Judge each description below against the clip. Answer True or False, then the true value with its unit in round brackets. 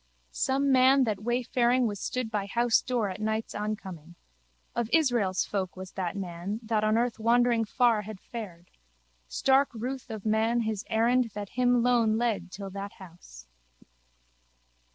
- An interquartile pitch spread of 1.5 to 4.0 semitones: True (3.5 semitones)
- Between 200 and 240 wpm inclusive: False (150 wpm)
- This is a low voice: False (220 Hz)